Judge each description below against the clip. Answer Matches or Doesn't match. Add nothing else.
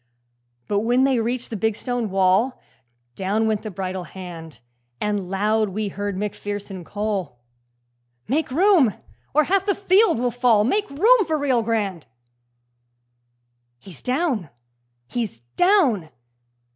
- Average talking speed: Doesn't match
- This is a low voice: Doesn't match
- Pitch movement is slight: Doesn't match